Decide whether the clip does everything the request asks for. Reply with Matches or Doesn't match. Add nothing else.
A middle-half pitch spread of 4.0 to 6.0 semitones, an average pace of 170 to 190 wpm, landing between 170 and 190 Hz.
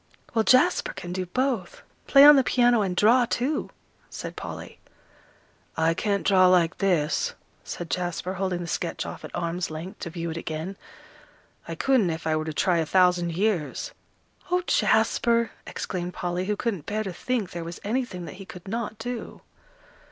Matches